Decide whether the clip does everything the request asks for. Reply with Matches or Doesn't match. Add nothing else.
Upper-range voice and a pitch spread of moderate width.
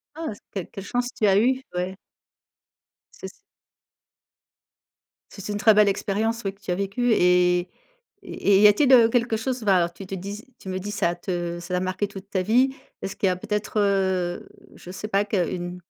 Matches